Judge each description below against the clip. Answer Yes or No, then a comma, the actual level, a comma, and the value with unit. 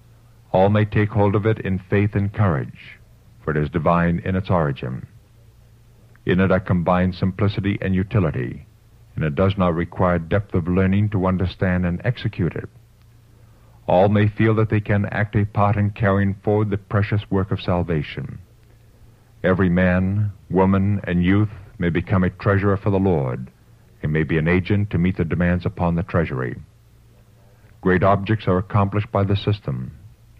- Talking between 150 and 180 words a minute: Yes, average, 170 wpm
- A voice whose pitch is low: Yes, low, 100 Hz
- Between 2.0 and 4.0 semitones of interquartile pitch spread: Yes, average, 3.2 semitones